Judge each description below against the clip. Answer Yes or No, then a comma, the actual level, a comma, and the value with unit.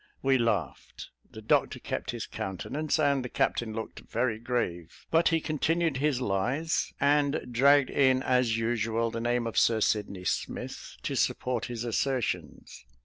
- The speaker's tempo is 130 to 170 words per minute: Yes, average, 150 wpm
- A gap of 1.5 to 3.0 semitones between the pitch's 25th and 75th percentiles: No, average, 3.7 semitones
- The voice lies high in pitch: No, low, 125 Hz